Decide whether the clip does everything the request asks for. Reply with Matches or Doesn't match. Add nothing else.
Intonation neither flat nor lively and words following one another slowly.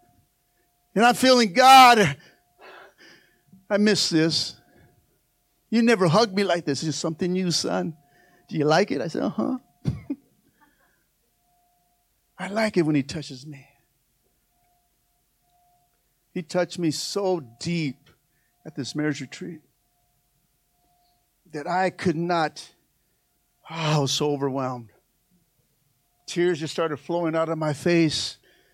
Matches